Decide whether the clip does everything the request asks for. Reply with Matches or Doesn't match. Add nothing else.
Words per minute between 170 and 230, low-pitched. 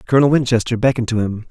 Matches